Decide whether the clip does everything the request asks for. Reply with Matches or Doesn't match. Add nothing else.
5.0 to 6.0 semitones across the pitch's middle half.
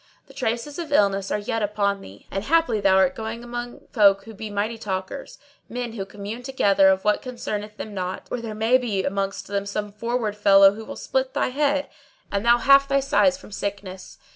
Doesn't match